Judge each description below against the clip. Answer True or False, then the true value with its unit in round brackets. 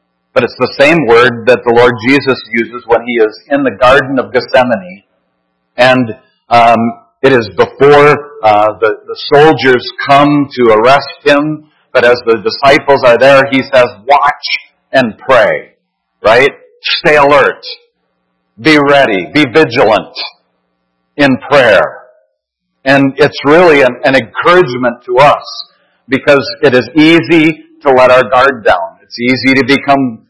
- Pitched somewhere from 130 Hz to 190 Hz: True (135 Hz)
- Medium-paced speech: True (145 wpm)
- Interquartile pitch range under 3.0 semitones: False (3.9 semitones)